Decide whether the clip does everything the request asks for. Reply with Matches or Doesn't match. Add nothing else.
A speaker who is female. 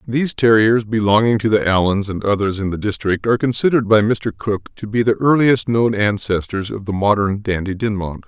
Doesn't match